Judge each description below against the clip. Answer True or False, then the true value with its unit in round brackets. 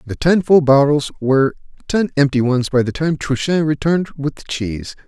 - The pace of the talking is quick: False (190 wpm)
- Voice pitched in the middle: True (145 Hz)